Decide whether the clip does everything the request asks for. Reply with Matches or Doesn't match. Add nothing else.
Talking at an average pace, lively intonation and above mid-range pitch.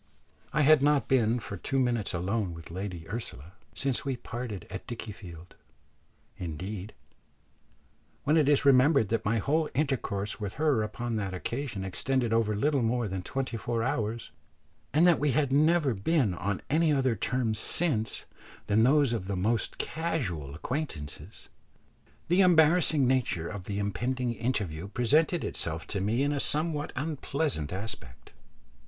Doesn't match